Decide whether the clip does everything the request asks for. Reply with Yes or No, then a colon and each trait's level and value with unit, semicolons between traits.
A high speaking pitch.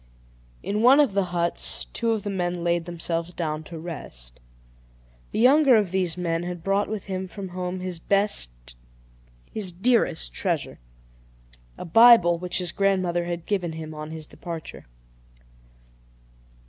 No: medium, 180 Hz